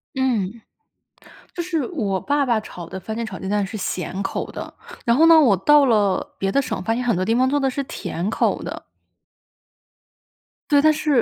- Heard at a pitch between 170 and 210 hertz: No, high, 235 Hz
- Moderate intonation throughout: No, wide, 6.3 semitones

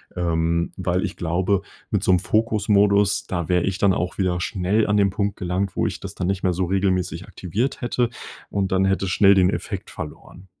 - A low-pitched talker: Yes, very low, 95 Hz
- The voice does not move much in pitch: Yes, narrow, 2.1 semitones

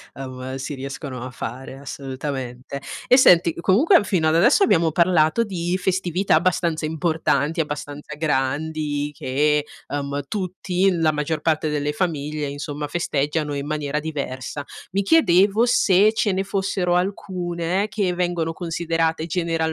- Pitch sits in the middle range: Yes, medium, 160 Hz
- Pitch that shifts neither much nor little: Yes, average, 3.8 semitones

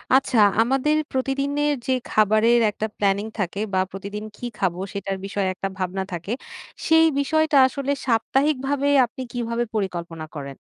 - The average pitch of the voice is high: Yes, high, 225 Hz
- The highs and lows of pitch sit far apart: Yes, wide, 5.9 semitones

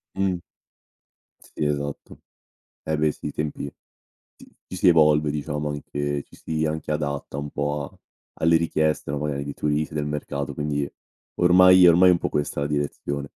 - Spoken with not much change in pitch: Yes, narrow, 1.5 semitones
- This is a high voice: No, very low, 75 Hz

